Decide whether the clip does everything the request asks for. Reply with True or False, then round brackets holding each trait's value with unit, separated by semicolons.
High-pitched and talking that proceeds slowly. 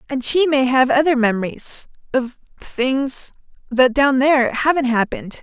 True (260 Hz; 120 wpm)